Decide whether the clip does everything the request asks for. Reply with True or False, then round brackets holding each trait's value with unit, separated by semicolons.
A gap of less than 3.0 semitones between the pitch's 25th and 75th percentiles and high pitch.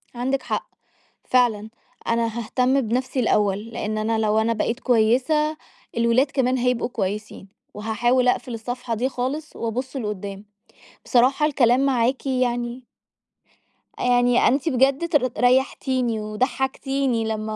True (2.6 semitones; 245 Hz)